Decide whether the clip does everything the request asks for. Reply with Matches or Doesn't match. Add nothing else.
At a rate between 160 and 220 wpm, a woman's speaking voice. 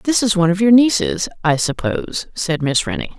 Matches